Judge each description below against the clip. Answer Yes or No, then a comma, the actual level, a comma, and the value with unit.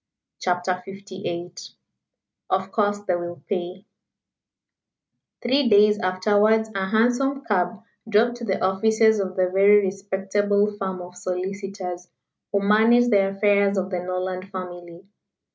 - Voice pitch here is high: Yes, high, 195 Hz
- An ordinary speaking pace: No, slow, 125 wpm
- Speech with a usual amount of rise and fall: No, narrow, 2.3 semitones